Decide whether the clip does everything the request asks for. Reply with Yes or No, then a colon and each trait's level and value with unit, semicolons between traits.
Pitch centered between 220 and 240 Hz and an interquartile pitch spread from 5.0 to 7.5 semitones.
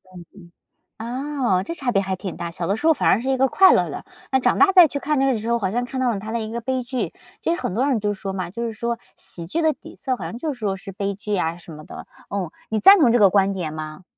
Yes: high, 225 Hz; average, 5.3 semitones